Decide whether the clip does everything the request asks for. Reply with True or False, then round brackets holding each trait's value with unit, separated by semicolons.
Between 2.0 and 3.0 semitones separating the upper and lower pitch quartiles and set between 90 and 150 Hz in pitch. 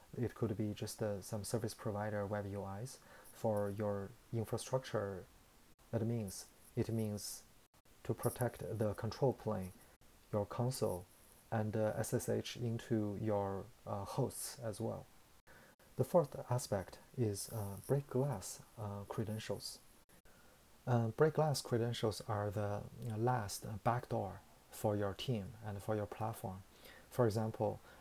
True (2.6 semitones; 110 Hz)